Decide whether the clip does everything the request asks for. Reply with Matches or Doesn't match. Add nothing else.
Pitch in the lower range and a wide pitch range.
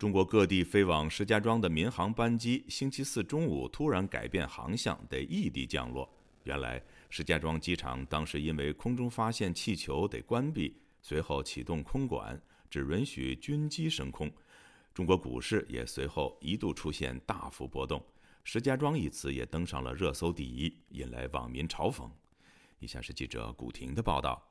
Matches